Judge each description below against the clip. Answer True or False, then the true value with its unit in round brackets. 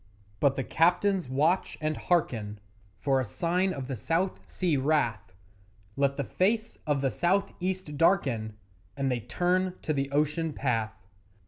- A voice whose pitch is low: False (150 Hz)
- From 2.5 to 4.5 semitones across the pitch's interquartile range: False (5.2 semitones)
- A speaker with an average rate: True (150 wpm)